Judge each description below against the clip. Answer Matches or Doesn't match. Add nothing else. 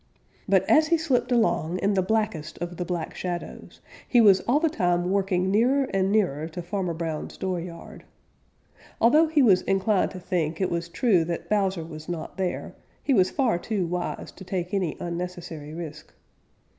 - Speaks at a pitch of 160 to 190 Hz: Matches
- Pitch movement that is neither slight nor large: Matches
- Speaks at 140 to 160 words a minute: Doesn't match